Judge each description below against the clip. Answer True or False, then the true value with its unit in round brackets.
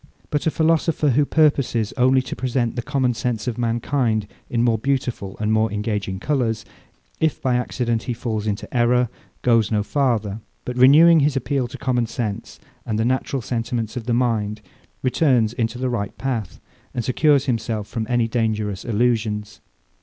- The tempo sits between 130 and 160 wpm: False (170 wpm)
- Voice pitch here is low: True (120 Hz)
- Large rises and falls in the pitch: False (2.9 semitones)